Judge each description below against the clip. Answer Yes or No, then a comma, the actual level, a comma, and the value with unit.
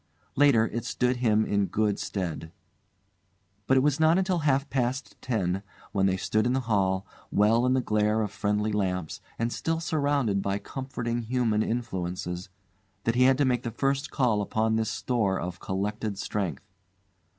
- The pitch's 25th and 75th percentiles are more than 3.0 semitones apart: Yes, average, 4.4 semitones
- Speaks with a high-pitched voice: No, low, 110 Hz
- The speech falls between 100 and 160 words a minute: No, average, 170 wpm